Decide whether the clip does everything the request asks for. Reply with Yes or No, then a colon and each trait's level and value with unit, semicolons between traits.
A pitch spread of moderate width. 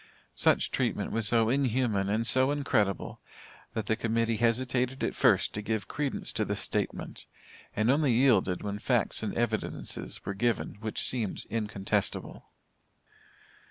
Yes: average, 3.1 semitones